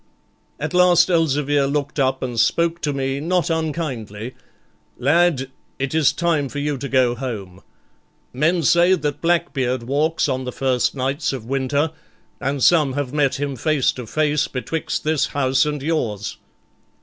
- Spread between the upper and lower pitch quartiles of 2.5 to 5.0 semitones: Yes, average, 3.3 semitones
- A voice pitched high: No, medium, 140 Hz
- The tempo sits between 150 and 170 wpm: Yes, average, 155 wpm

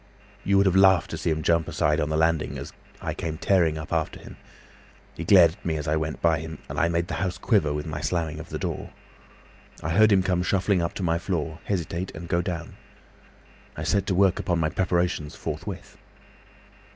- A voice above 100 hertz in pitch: No, very low, 85 Hz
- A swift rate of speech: Yes, fast, 210 wpm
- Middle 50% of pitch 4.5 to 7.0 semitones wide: No, average, 2.8 semitones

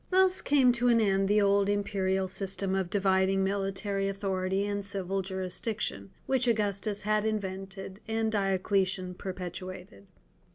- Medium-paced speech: No, slow, 130 wpm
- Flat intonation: Yes, narrow, 1.6 semitones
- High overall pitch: Yes, high, 195 Hz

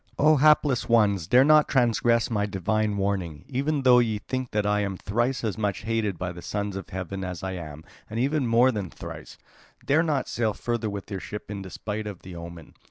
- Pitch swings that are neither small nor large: Yes, average, 4.2 semitones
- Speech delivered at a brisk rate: Yes, fast, 220 wpm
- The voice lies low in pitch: Yes, low, 105 Hz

